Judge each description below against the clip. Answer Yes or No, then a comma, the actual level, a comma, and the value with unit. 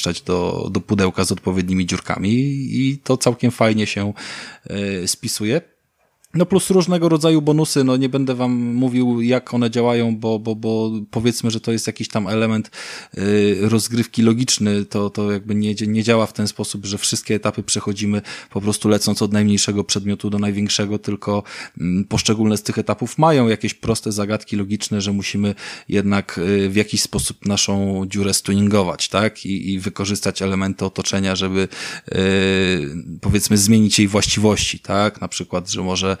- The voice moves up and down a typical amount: No, narrow, 2.3 semitones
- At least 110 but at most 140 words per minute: No, average, 155 wpm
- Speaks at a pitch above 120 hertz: No, low, 105 Hz